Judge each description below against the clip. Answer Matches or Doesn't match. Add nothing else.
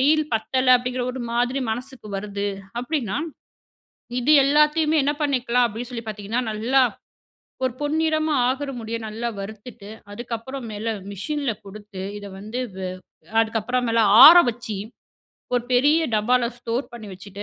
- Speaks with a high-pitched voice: Matches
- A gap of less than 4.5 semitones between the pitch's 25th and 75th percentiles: Matches